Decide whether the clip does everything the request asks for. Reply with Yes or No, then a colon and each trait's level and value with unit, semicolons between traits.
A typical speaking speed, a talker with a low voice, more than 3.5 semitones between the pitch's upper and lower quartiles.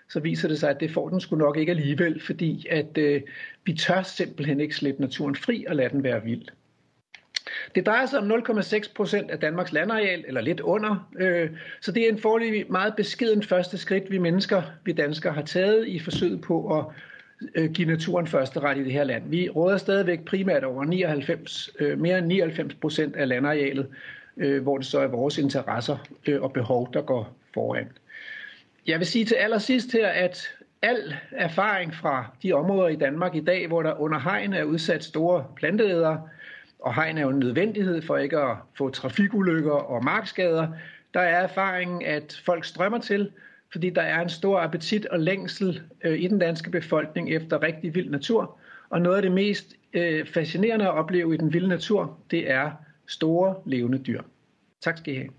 No: average, 190 wpm; medium, 175 Hz; average, 4.0 semitones